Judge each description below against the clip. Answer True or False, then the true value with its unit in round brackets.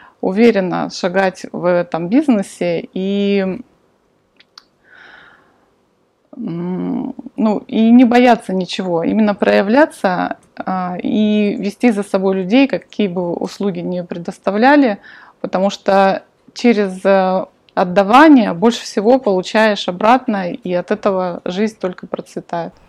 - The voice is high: True (200 Hz)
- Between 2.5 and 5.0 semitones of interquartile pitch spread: True (4.2 semitones)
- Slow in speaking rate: True (95 wpm)